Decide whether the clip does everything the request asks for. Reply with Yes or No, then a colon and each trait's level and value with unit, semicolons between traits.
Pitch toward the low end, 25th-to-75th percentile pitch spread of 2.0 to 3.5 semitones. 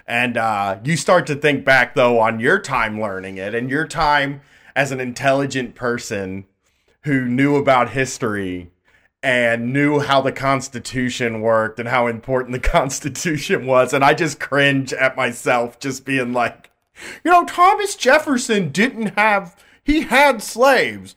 No: low, 130 Hz; average, 3.9 semitones